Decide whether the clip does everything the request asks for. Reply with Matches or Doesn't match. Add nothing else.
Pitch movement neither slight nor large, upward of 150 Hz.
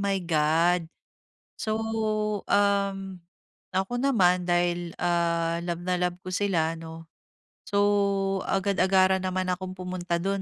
Doesn't match